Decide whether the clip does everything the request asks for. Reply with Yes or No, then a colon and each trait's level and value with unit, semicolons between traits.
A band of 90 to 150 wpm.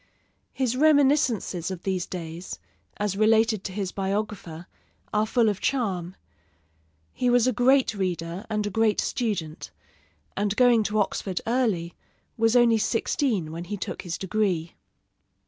Yes: average, 140 wpm